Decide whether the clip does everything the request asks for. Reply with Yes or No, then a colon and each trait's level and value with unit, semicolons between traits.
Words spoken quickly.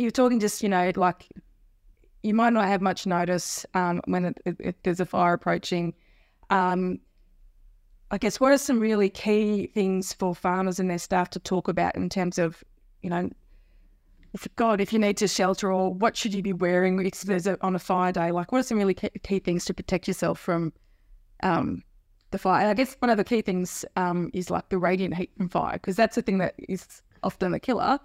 Yes: fast, 215 wpm